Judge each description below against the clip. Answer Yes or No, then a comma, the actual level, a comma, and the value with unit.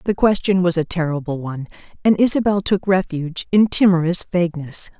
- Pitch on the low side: No, medium, 180 Hz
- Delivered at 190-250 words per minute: No, average, 155 wpm